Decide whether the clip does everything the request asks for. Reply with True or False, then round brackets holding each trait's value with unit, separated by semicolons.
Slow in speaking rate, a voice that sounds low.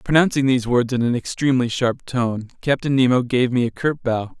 False (205 wpm; 125 Hz)